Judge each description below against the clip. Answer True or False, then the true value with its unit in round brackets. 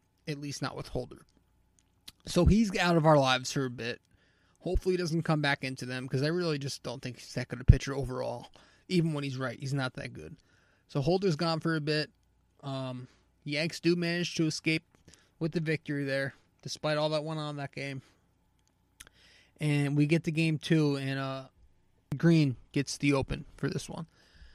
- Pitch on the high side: False (140 Hz)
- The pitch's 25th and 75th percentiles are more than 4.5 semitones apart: False (3.7 semitones)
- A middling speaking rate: True (195 wpm)